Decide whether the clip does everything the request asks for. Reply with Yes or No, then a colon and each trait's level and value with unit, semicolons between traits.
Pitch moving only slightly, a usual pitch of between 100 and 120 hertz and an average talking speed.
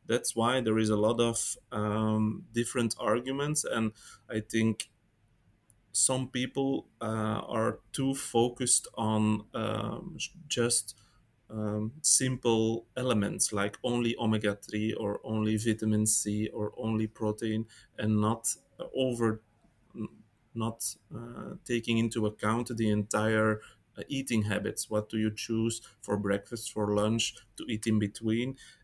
No: narrow, 1.7 semitones; low, 110 Hz; slow, 125 wpm